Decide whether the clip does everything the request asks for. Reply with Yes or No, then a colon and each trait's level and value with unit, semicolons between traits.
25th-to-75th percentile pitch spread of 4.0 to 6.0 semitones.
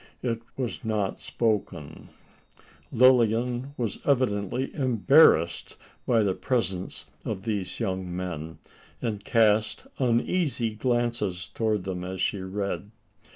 Yes: average, 4.3 semitones